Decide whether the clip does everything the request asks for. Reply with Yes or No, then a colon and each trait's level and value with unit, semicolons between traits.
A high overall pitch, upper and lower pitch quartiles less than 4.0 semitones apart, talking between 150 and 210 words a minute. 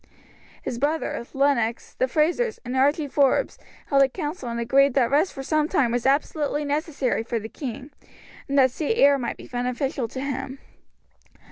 Yes: very high, 275 Hz; average, 2.9 semitones; average, 170 wpm